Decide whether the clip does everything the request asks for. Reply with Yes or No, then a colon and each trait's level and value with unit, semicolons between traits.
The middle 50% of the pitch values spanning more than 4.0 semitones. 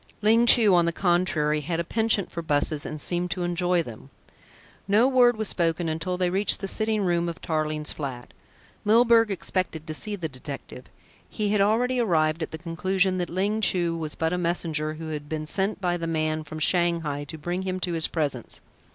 No: average, 3.7 semitones